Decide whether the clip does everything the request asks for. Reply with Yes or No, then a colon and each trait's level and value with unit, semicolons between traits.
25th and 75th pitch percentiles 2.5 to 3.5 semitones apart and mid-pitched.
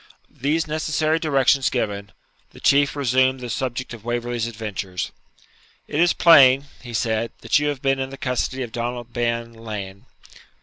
No: average, 3.0 semitones; low, 125 Hz